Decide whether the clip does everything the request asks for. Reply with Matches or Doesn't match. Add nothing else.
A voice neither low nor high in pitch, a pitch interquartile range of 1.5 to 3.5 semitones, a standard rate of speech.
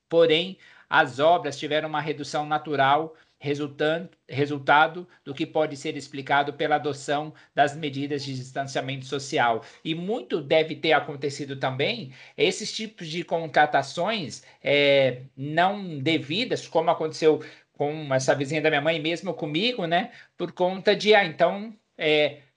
Matches